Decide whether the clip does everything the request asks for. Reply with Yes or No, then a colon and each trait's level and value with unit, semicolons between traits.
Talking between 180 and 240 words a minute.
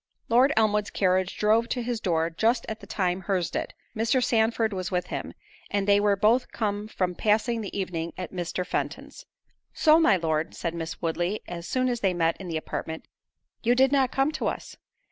Yes: average, 200 wpm